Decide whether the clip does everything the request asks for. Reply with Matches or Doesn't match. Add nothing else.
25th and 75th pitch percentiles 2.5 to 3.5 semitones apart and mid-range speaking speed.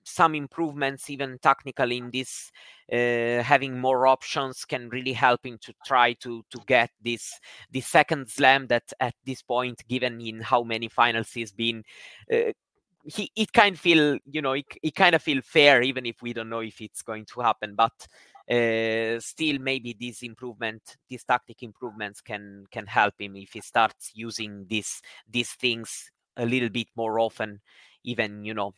Matches